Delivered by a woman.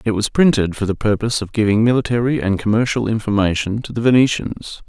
No: male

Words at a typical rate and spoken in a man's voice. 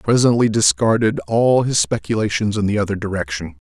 Yes: average, 165 wpm; male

